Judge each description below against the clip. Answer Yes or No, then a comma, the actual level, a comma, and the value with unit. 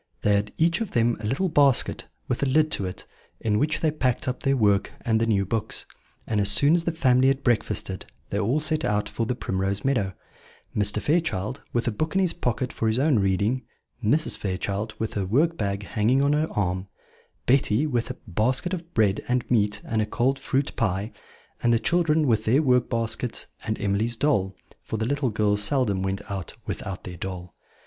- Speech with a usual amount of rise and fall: Yes, average, 5.0 semitones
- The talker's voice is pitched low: Yes, low, 115 Hz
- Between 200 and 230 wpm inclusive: Yes, fast, 205 wpm